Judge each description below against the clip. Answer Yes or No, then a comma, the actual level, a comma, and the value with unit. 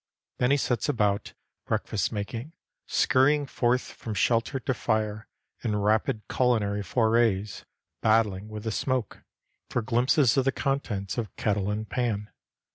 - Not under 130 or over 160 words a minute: Yes, slow, 135 wpm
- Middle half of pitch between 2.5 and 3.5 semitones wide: Yes, average, 3.2 semitones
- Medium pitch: No, low, 110 Hz